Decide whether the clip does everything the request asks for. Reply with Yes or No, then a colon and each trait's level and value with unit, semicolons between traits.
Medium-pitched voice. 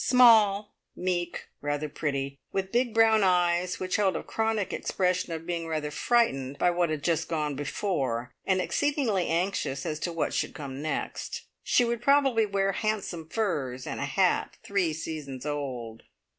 Yes: medium, 175 Hz